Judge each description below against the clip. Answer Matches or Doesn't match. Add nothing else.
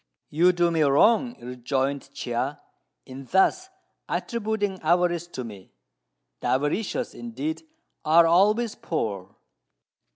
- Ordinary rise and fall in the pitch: Doesn't match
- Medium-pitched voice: Matches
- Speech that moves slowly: Matches